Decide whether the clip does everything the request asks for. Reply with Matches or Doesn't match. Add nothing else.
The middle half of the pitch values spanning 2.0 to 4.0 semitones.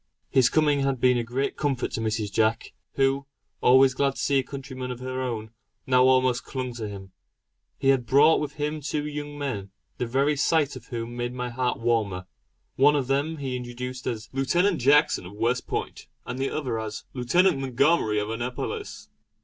Matches